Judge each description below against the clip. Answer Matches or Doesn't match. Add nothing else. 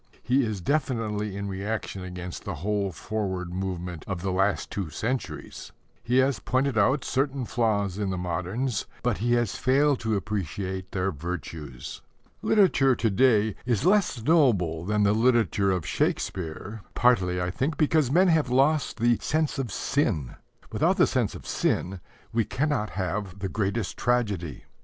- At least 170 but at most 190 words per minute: Doesn't match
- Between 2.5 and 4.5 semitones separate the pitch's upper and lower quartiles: Doesn't match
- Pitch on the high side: Doesn't match